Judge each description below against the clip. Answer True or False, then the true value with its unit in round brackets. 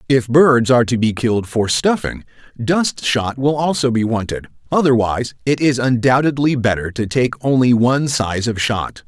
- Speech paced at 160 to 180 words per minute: True (170 wpm)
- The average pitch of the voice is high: False (125 Hz)